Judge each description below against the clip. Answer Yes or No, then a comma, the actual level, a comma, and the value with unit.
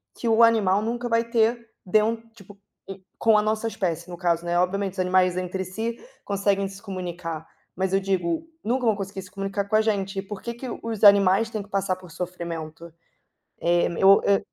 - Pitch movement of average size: Yes, average, 3.0 semitones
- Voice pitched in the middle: No, high, 195 Hz